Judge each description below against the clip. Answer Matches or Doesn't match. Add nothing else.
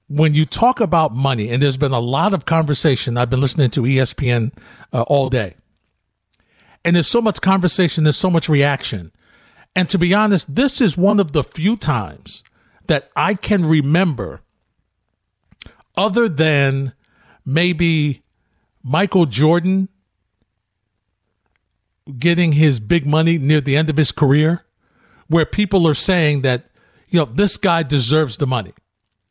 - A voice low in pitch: Doesn't match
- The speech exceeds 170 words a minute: Doesn't match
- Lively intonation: Matches